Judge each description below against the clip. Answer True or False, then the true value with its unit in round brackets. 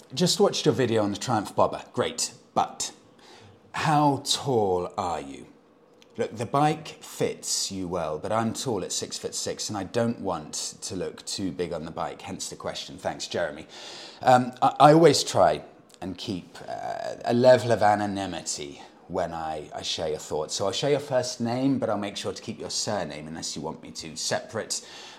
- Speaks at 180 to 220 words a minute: True (195 wpm)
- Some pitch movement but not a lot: False (5.8 semitones)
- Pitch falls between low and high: False (120 Hz)